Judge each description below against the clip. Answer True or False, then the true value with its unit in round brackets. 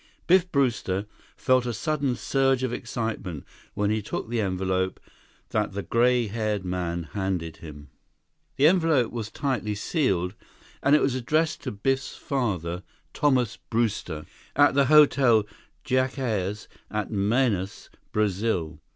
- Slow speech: True (130 wpm)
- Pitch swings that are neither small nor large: False (5.7 semitones)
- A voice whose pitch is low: True (110 Hz)